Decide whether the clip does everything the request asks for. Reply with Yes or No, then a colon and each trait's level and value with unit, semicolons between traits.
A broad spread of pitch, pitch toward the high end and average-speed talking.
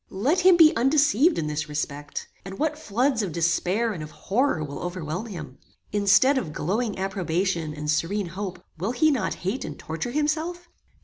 Yes: wide, 8.4 semitones; high, 195 Hz; average, 175 wpm